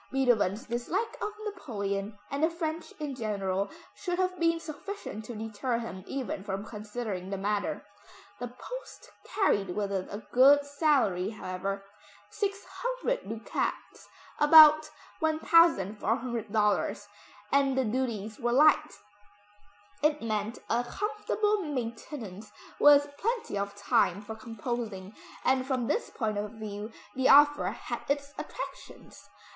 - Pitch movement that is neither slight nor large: No, wide, 6.6 semitones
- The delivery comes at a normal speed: No, slow, 125 wpm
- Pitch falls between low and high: No, high, 240 Hz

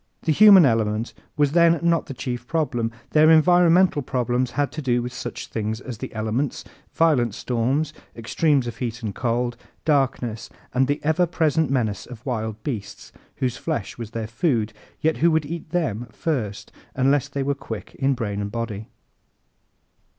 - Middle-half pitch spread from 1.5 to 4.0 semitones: No, average, 5.1 semitones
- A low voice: Yes, low, 130 Hz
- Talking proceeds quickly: No, average, 165 wpm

